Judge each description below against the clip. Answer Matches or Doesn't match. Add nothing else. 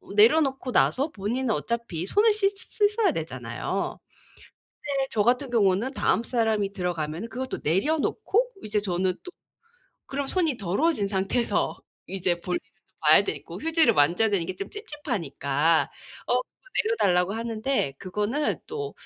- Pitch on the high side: Matches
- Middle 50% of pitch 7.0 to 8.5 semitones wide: Matches